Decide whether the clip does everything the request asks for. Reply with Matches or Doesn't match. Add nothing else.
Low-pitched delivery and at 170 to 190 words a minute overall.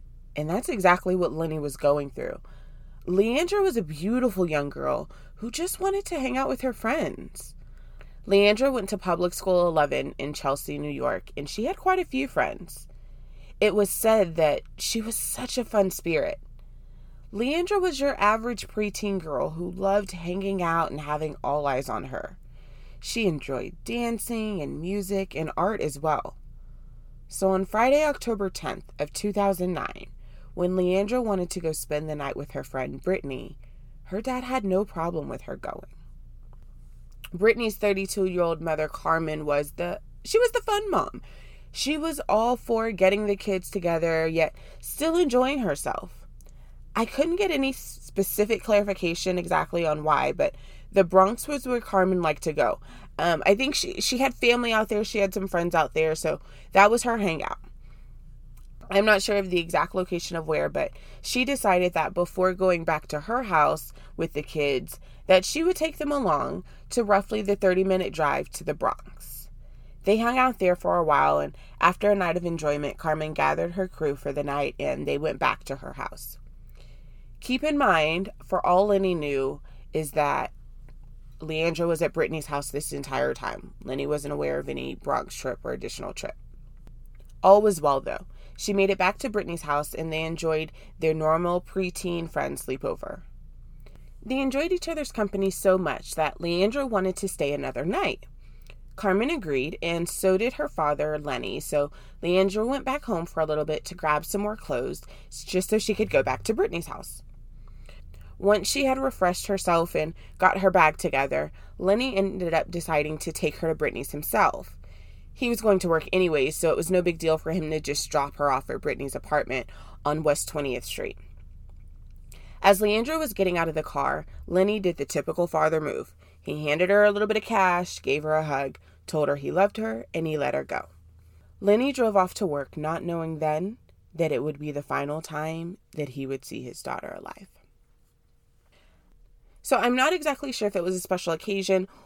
Doesn't match